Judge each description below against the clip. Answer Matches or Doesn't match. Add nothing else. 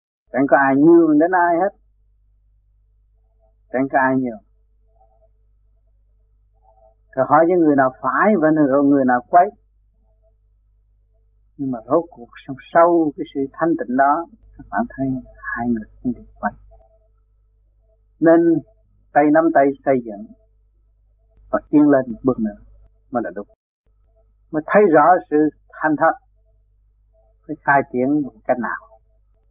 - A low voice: Matches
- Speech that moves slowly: Matches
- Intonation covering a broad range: Doesn't match